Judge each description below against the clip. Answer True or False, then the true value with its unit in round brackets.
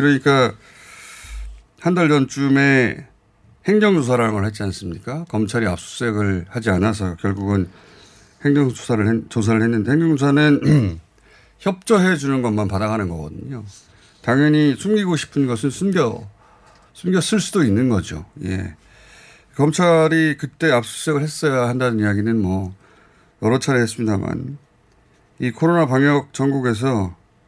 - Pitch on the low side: True (120 Hz)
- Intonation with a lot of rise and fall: True (6.2 semitones)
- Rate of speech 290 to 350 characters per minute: False (280 characters per minute)